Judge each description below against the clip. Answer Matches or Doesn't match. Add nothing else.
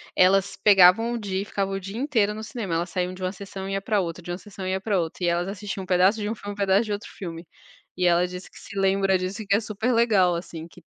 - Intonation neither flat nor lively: Doesn't match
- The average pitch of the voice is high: Matches